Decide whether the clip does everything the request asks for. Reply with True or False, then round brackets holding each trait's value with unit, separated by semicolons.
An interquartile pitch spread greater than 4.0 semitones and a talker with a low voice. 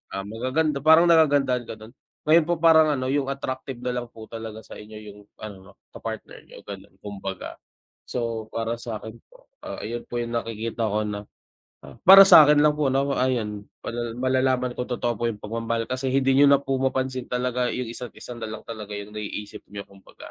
False (3.4 semitones; 120 Hz)